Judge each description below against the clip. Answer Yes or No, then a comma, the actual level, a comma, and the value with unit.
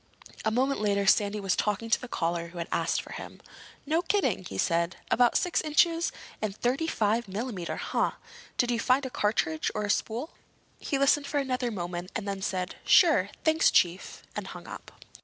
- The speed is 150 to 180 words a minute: No, average, 190 wpm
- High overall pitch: Yes, high, 220 Hz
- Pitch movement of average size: No, wide, 6.2 semitones